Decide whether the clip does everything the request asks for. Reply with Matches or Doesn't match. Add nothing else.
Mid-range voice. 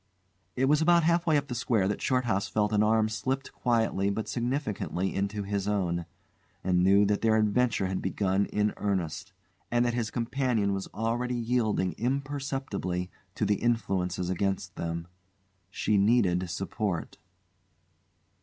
Doesn't match